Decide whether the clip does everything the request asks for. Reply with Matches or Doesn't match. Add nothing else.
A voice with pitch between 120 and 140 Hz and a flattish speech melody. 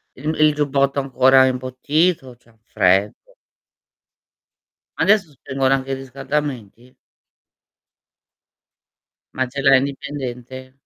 Matches